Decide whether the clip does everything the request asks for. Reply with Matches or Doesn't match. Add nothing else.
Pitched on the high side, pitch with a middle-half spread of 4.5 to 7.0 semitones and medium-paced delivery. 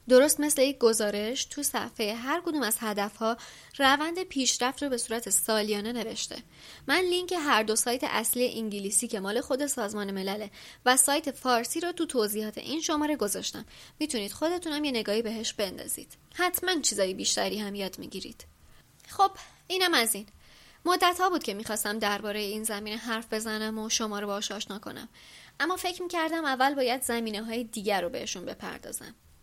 Doesn't match